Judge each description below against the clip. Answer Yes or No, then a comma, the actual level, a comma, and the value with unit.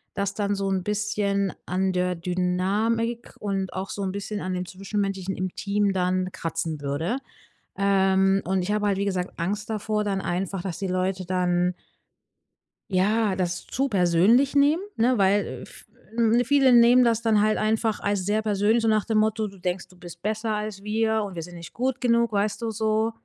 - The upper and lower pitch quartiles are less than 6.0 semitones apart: Yes, average, 2.8 semitones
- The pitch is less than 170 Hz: No, high, 200 Hz